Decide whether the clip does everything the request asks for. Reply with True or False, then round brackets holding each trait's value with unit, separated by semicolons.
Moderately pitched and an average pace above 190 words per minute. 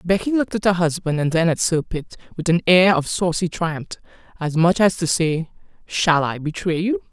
True (170 Hz; 200 wpm)